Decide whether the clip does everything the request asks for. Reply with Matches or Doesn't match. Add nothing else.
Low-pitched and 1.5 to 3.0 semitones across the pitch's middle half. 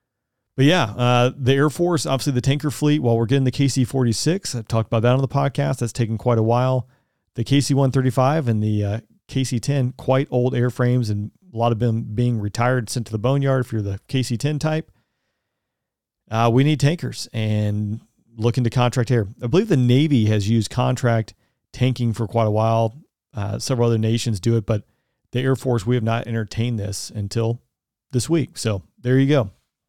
Matches